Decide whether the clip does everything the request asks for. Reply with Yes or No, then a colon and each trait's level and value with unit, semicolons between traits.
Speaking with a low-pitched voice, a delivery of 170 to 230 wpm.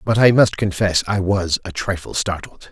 Yes: very low, 95 Hz; average, 200 wpm